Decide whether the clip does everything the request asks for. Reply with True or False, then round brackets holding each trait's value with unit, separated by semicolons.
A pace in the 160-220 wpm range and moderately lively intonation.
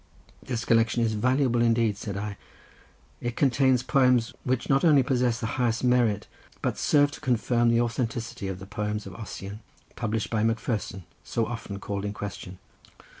True (165 wpm; 3.0 semitones)